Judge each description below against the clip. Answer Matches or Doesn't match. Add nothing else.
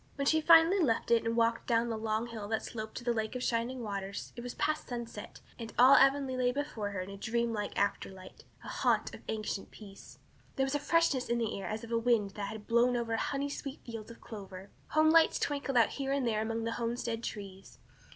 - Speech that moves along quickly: Matches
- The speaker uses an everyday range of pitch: Matches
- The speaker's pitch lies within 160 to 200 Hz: Doesn't match